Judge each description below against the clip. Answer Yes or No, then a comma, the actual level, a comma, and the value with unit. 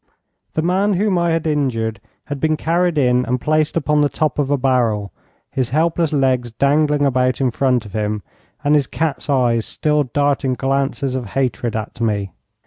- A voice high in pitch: No, low, 135 Hz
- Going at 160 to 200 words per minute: Yes, average, 180 wpm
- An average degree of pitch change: Yes, average, 3.6 semitones